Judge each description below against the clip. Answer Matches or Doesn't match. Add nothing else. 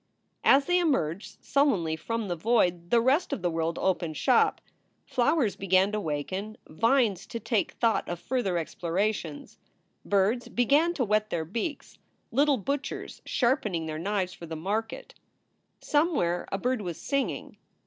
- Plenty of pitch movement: Matches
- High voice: Matches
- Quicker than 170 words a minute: Doesn't match